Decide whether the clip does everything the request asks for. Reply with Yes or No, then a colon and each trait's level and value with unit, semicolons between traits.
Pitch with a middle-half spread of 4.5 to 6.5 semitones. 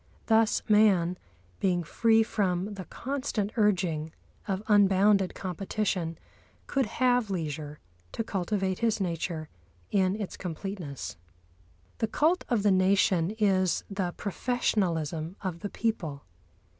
No: average, 3.4 semitones